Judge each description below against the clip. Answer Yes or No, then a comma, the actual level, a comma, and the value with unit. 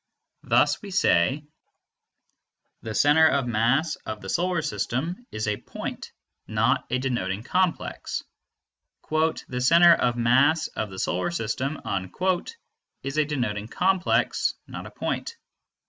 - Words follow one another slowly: Yes, slow, 125 wpm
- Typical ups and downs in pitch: No, wide, 6.6 semitones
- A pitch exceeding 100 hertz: Yes, low, 135 Hz